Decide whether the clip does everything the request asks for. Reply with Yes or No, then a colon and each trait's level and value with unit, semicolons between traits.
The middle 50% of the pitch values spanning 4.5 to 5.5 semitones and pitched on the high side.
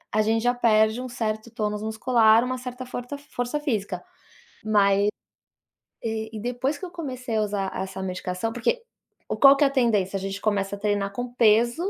No: average, 3.3 semitones; high, 225 Hz